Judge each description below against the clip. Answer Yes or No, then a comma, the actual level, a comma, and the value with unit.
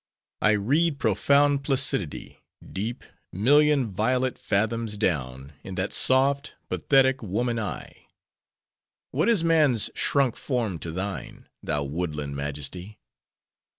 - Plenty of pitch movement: Yes, wide, 6.9 semitones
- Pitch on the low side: Yes, low, 110 Hz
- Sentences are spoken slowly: Yes, slow, 100 wpm